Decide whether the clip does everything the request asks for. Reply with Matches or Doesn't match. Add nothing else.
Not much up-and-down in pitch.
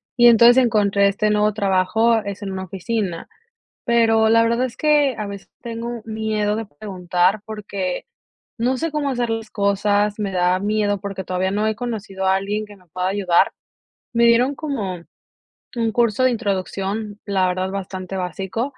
Doesn't match